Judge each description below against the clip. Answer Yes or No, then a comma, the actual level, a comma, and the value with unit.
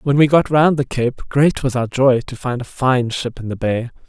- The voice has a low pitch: Yes, low, 130 Hz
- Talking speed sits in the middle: No, fast, 265 wpm